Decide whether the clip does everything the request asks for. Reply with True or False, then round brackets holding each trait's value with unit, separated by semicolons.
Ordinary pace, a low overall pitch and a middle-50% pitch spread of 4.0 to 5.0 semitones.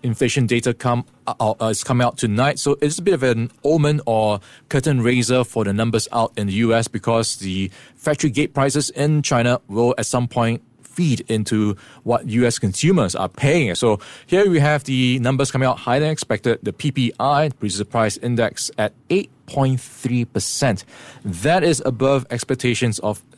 False (180 wpm; 125 Hz; 3.1 semitones)